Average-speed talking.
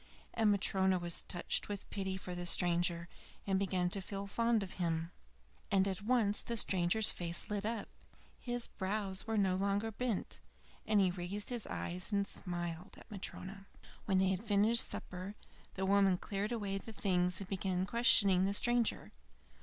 Yes: average, 165 wpm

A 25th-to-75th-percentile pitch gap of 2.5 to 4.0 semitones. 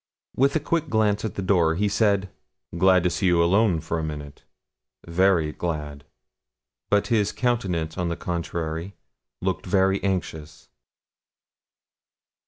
Yes: average, 3.6 semitones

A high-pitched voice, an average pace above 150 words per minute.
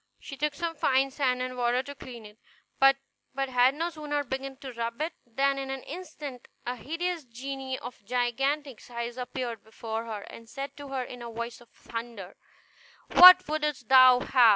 Yes: very high, 260 Hz; average, 180 wpm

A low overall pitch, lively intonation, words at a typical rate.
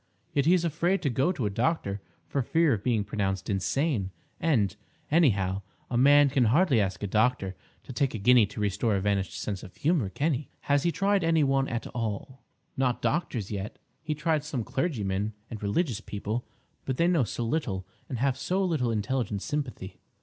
Yes: low, 125 Hz; wide, 6.6 semitones; average, 195 wpm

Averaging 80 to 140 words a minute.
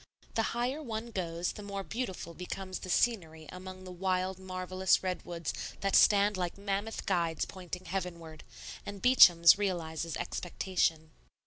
Yes: slow, 135 wpm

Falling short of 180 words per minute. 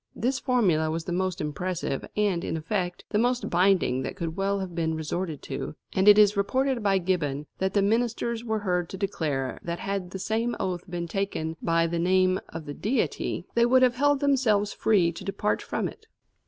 No: average, 200 wpm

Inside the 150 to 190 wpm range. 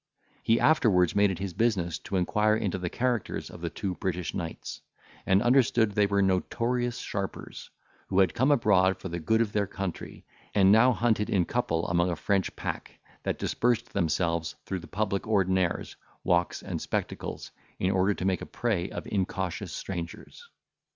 Yes: average, 170 wpm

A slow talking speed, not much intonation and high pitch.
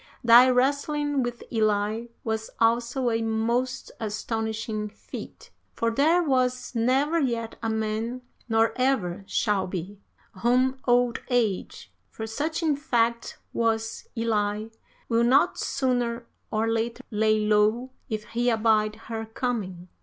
Yes: slow, 125 wpm; narrow, 2.3 semitones; high, 230 Hz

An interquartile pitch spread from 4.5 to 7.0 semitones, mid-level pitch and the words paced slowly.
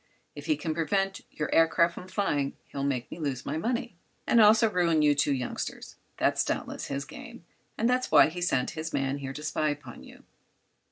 No: average, 5.2 semitones; medium, 160 Hz; average, 190 wpm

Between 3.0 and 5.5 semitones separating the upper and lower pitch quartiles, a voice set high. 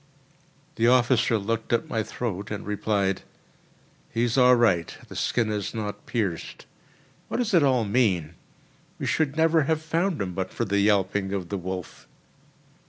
No: average, 4.3 semitones; low, 110 Hz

